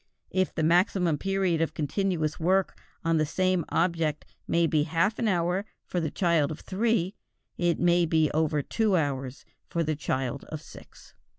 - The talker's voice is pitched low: No, medium, 170 Hz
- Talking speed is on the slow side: No, average, 170 wpm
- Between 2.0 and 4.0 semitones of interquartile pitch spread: Yes, average, 3.1 semitones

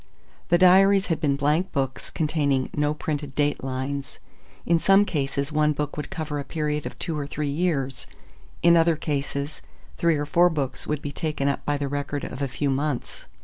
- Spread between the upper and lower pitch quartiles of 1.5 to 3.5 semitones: Yes, narrow, 2.4 semitones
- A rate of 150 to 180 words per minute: No, average, 190 wpm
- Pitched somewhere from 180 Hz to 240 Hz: No, medium, 150 Hz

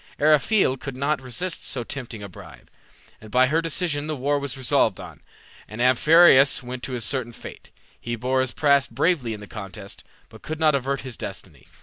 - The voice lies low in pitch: Yes, low, 130 Hz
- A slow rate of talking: No, average, 195 wpm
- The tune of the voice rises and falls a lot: No, average, 3.5 semitones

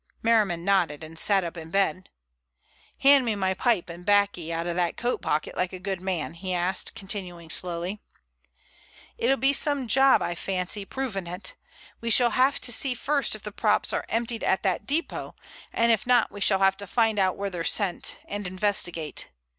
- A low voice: No, high, 195 Hz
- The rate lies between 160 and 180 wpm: No, average, 190 wpm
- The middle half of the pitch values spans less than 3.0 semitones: No, average, 4.3 semitones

